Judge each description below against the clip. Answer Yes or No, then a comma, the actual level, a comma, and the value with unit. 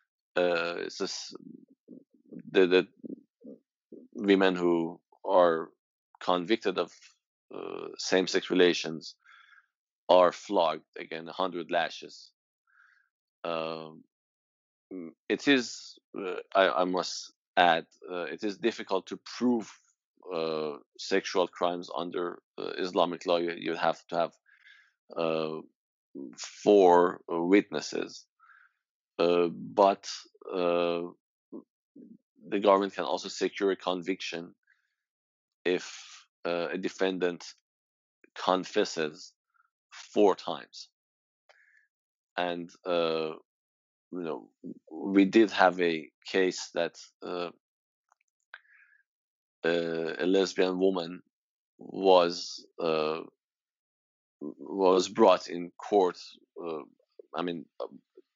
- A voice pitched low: Yes, very low, 90 Hz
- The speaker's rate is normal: No, slow, 90 wpm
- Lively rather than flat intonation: No, narrow, 2.6 semitones